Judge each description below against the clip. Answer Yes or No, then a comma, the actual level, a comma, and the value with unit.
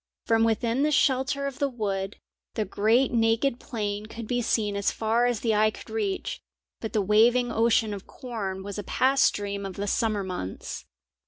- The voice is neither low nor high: No, high, 225 Hz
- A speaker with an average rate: Yes, average, 185 wpm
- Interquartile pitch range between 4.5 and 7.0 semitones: No, average, 3.2 semitones